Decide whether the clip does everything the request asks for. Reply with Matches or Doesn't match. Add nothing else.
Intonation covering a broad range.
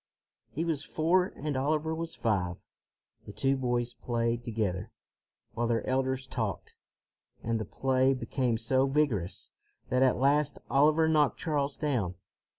Doesn't match